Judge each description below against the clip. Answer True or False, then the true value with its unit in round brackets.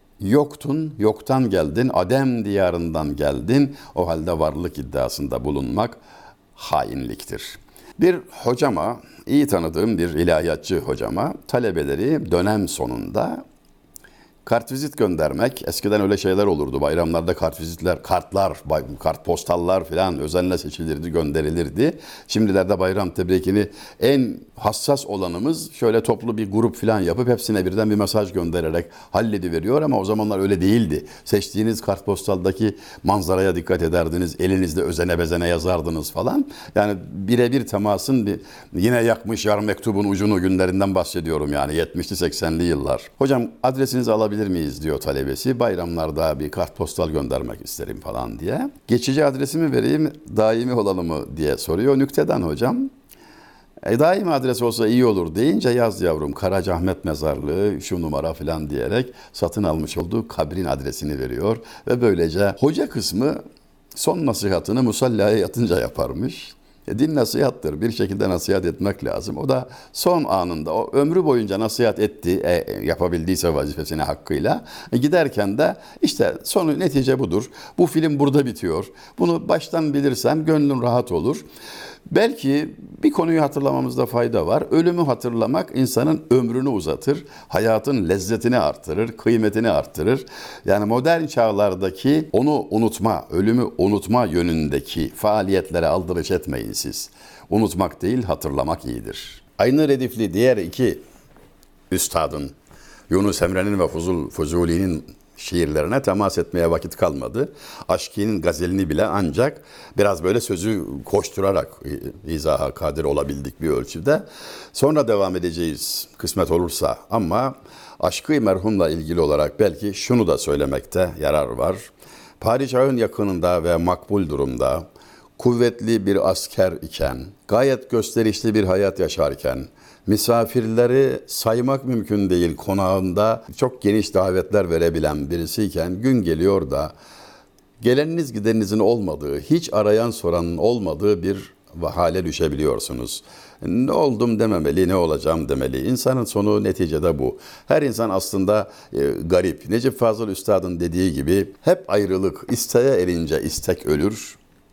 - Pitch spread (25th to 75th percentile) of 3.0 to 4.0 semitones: False (5.5 semitones)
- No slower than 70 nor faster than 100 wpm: False (125 wpm)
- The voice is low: True (105 Hz)